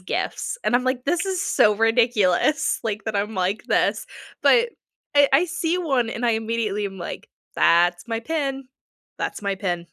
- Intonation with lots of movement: Yes, wide, 5.7 semitones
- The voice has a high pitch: Yes, high, 230 Hz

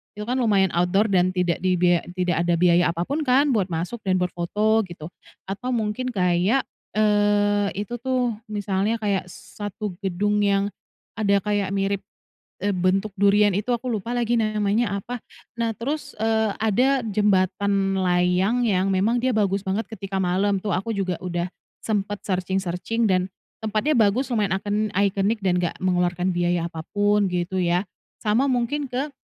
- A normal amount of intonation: Yes, average, 3.0 semitones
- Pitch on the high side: Yes, high, 200 Hz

